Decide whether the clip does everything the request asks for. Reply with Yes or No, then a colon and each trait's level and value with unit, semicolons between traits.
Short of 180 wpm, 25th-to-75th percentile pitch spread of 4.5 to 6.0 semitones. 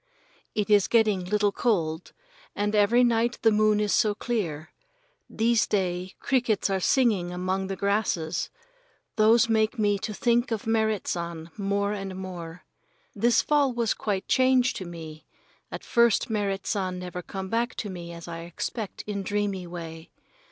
No: average, 160 wpm; average, 3.7 semitones